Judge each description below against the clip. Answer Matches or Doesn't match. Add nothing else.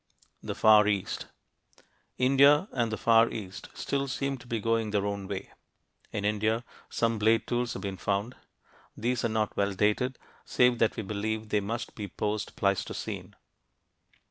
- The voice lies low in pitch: Matches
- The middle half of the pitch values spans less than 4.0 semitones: Matches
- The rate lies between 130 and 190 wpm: Matches